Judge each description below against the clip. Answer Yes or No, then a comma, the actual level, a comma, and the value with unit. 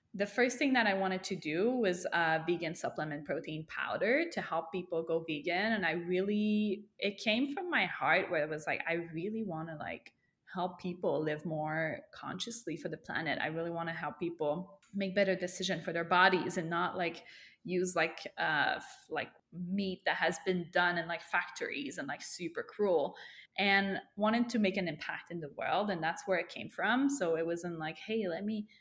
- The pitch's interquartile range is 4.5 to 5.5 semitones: No, average, 3.5 semitones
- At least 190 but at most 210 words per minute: Yes, fast, 205 wpm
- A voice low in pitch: No, medium, 180 Hz